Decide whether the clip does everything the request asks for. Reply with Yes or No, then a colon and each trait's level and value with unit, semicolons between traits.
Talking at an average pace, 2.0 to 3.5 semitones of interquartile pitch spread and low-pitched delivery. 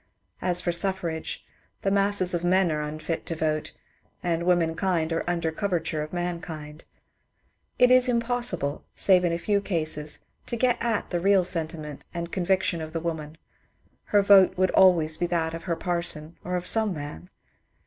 No: average, 170 wpm; average, 2.9 semitones; medium, 175 Hz